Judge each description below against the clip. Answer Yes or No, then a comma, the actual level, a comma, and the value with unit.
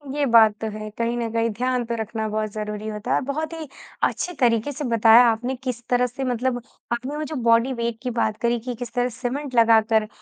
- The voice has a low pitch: No, high, 235 Hz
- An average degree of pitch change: No, narrow, 2.3 semitones